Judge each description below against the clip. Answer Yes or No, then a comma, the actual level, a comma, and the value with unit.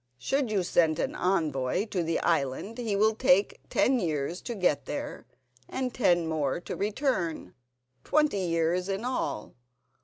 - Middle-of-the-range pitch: Yes, medium, 180 Hz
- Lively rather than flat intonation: Yes, wide, 6.1 semitones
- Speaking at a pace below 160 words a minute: Yes, average, 145 wpm